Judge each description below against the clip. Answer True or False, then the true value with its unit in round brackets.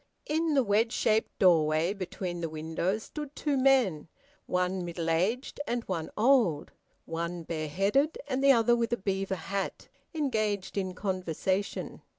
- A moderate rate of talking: True (145 wpm)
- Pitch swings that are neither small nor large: False (5.7 semitones)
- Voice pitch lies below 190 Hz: False (195 Hz)